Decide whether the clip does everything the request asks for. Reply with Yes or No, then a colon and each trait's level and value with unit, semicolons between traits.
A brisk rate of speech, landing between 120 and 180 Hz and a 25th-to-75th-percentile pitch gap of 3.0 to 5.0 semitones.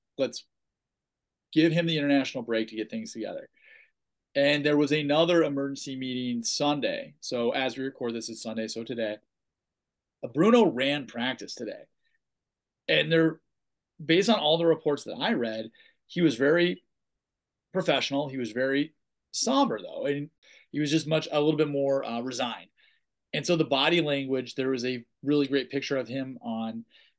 No: average, 165 wpm; medium, 140 Hz; average, 4.2 semitones